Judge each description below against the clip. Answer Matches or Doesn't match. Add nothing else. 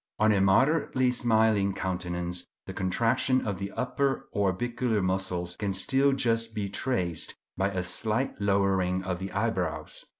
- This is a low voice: Matches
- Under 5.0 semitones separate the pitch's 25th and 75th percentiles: Matches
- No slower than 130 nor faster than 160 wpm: Matches